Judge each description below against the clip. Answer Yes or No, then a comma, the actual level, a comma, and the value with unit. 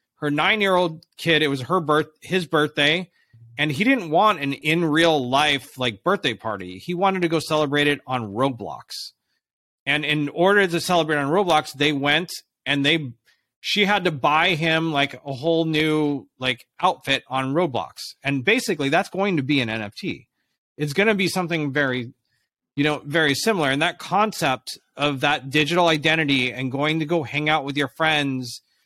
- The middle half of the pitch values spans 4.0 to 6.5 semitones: No, average, 3.5 semitones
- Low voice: No, medium, 150 Hz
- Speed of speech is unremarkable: Yes, average, 180 wpm